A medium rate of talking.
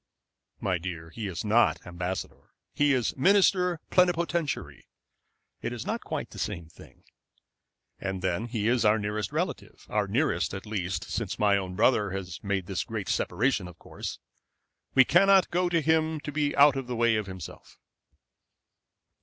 Yes: average, 160 wpm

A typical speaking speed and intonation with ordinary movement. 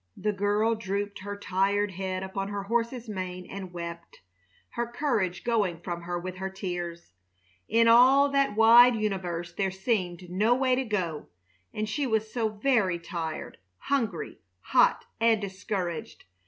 Yes: average, 150 wpm; average, 3.9 semitones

